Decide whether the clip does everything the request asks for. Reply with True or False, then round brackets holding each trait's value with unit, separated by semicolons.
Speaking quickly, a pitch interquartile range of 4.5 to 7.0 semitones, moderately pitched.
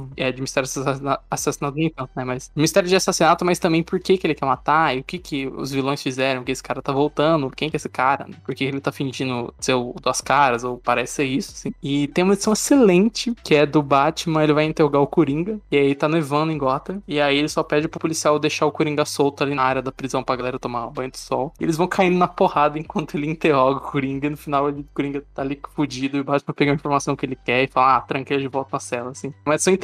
False (255 wpm; 2.9 semitones; 145 Hz)